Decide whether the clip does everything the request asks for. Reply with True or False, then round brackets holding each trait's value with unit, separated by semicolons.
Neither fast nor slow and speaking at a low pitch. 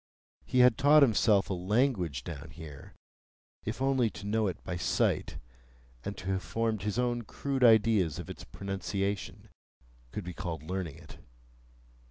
True (150 wpm; 100 Hz)